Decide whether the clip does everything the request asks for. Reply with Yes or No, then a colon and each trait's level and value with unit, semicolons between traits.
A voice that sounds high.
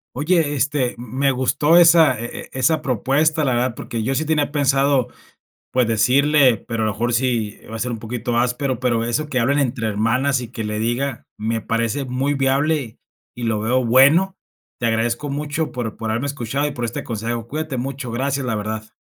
No: low, 125 Hz